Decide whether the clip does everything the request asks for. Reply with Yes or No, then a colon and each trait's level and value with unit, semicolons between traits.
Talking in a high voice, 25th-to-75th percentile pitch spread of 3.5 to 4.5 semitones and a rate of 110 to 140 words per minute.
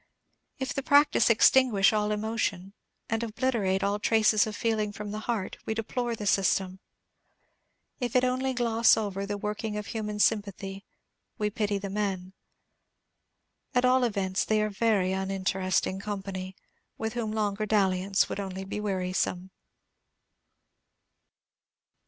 No: high, 210 Hz; narrow, 2.5 semitones; slow, 135 wpm